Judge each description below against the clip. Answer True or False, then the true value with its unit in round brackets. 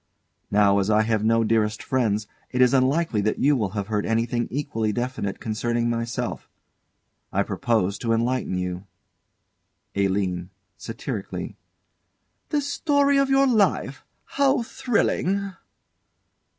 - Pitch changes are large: True (5.7 semitones)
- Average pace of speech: False (125 wpm)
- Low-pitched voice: True (115 Hz)